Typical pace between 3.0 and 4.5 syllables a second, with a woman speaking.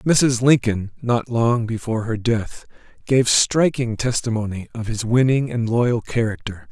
No: 4.2 syllables/s; male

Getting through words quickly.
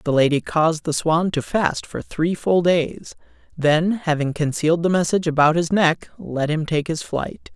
No: average, 190 wpm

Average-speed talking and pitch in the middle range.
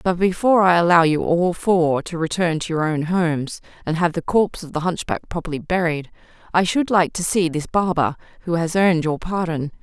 No: fast, 210 wpm; medium, 170 Hz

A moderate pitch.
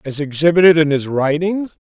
Yes: medium, 160 Hz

